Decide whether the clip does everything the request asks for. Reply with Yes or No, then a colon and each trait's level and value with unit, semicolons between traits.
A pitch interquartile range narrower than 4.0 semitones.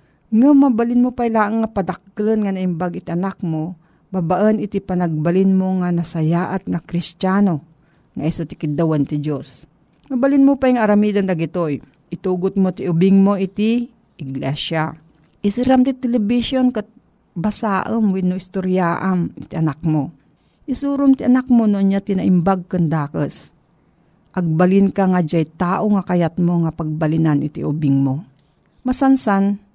No: average, 4.5 semitones